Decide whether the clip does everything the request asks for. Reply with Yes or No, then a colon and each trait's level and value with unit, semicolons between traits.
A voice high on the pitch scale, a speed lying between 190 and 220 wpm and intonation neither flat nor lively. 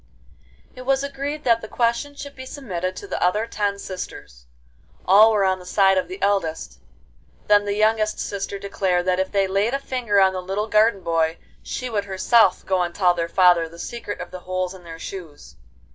Yes: high, 195 Hz; fast, 205 wpm; average, 3.6 semitones